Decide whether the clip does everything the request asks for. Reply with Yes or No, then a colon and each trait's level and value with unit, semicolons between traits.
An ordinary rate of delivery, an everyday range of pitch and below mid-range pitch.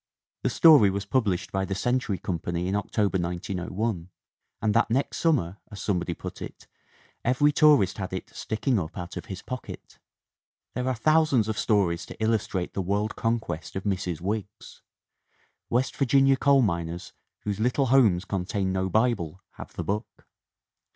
Yes: average, 165 wpm; average, 4.9 semitones; low, 100 Hz